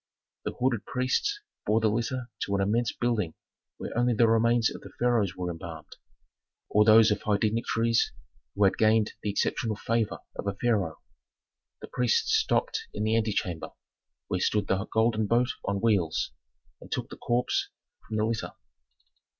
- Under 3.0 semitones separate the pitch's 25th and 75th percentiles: Yes, narrow, 2.5 semitones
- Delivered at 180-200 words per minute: No, average, 160 wpm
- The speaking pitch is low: Yes, low, 110 Hz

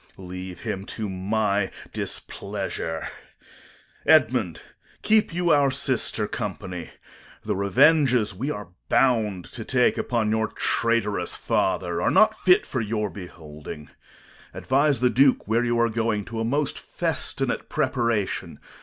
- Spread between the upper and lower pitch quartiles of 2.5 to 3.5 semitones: No, average, 4.7 semitones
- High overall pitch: No, low, 110 Hz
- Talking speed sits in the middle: No, slow, 130 wpm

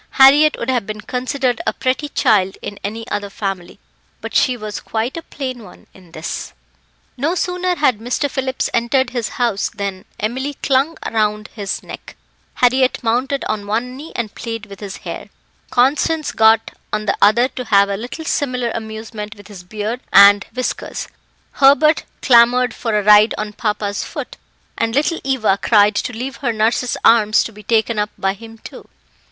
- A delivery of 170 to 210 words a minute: Yes, average, 175 wpm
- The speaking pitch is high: Yes, high, 230 Hz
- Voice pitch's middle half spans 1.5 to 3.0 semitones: No, average, 3.6 semitones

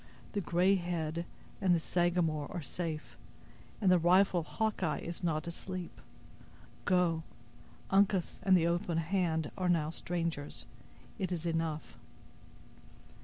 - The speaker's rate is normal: No, slow, 120 wpm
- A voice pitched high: No, medium, 170 Hz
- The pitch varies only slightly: Yes, narrow, 2.1 semitones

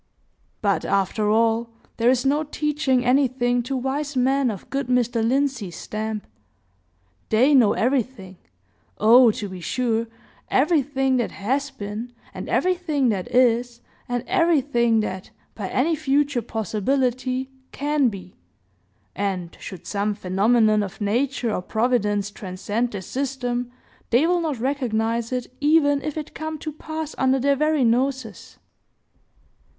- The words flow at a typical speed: No, slow, 130 wpm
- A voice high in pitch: Yes, high, 245 Hz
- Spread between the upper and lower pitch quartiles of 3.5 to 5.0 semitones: Yes, average, 4.3 semitones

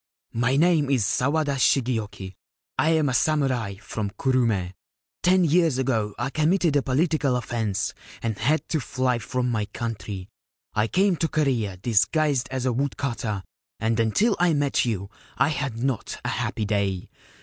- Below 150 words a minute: No, average, 160 wpm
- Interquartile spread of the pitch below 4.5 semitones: No, average, 5.0 semitones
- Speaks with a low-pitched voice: Yes, low, 125 Hz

